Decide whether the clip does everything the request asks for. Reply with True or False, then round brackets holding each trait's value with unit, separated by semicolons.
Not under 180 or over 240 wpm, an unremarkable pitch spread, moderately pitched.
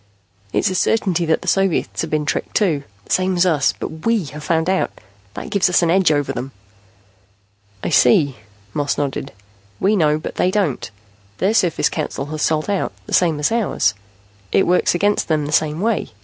True (190 wpm; 4.0 semitones; 165 Hz)